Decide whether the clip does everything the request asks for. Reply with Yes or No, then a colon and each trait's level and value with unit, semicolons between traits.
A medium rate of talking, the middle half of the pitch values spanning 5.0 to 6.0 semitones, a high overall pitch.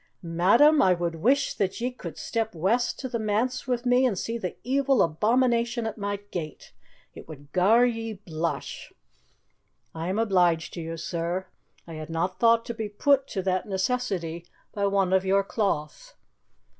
Yes: average, 170 wpm; wide, 5.5 semitones; high, 200 Hz